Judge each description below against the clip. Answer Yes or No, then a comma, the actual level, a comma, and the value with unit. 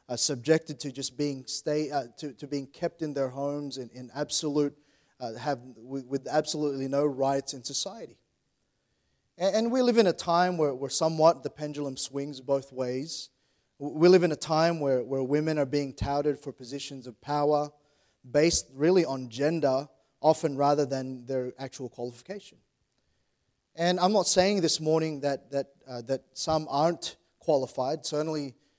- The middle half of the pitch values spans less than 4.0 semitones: Yes, narrow, 2.6 semitones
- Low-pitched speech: No, medium, 145 Hz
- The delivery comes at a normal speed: Yes, average, 165 wpm